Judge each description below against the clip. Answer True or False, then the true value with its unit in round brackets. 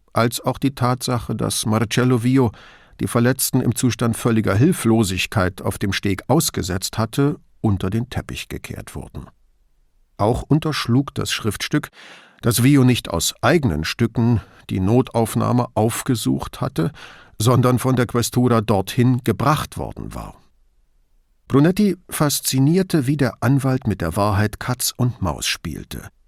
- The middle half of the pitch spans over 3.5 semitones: False (3.1 semitones)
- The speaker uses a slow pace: True (130 wpm)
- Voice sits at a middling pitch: False (120 Hz)